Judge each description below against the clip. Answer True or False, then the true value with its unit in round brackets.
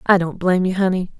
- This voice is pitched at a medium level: True (180 Hz)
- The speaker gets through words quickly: True (250 wpm)